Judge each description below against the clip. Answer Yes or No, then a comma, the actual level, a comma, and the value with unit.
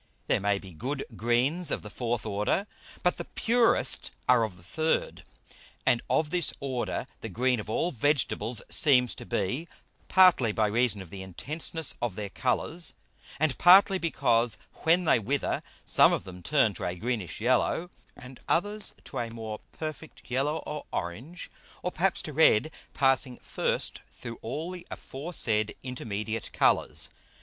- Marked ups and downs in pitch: Yes, wide, 6.4 semitones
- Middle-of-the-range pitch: No, low, 125 Hz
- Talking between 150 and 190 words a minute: Yes, average, 160 wpm